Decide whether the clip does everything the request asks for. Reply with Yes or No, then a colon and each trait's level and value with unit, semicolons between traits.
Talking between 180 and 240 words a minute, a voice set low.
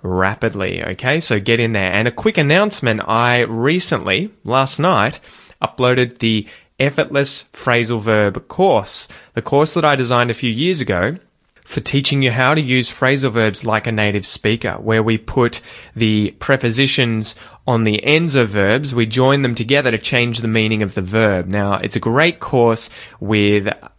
No: average, 170 wpm; low, 120 Hz